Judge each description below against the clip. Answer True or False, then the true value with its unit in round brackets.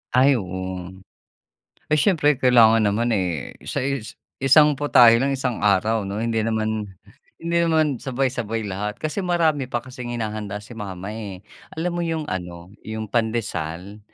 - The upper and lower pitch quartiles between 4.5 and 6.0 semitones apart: True (4.9 semitones)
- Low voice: True (115 Hz)